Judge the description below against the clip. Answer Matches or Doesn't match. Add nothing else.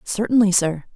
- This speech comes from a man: Doesn't match